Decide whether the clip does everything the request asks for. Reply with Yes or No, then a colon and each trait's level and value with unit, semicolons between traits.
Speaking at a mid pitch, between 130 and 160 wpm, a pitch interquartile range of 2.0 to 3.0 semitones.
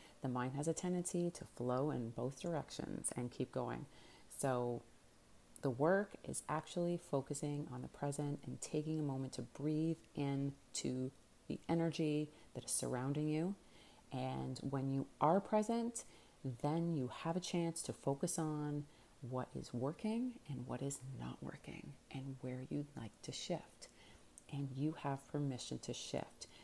No: medium, 145 Hz; average, 155 wpm; average, 4.0 semitones